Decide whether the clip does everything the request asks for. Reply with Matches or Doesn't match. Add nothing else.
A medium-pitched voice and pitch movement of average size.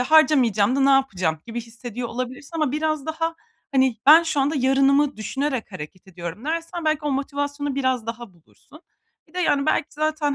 Doesn't match